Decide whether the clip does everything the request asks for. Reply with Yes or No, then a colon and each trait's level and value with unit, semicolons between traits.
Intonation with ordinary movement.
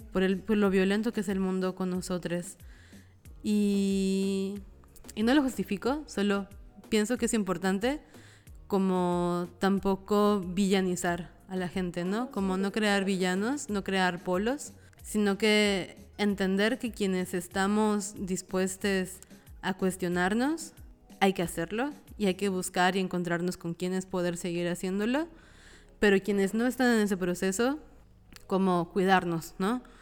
No: narrow, 2.3 semitones